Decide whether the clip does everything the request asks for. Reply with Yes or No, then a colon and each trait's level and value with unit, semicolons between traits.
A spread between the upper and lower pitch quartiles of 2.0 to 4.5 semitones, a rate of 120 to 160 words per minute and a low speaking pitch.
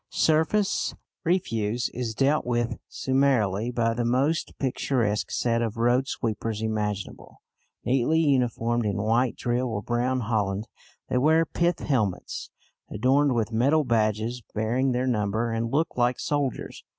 Yes: average, 3.2 semitones; slow, 135 wpm; low, 120 Hz